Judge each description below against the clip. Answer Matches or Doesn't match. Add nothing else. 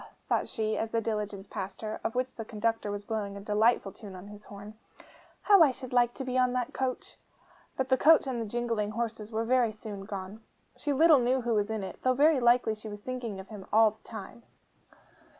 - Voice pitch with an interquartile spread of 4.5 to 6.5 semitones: Doesn't match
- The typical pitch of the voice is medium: Doesn't match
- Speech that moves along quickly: Matches